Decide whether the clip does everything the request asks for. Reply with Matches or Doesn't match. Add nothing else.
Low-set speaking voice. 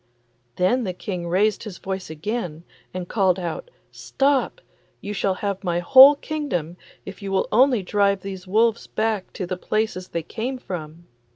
Doesn't match